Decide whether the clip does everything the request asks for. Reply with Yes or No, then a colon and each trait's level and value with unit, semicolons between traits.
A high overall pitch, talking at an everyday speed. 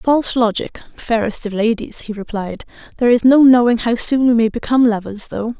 Yes: high, 230 Hz; average, 195 wpm